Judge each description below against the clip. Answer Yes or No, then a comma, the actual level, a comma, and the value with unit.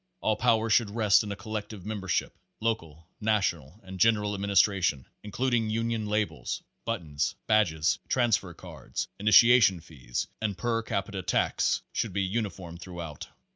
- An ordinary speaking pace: Yes, average, 145 wpm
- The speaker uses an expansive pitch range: No, average, 3.7 semitones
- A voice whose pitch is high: No, low, 105 Hz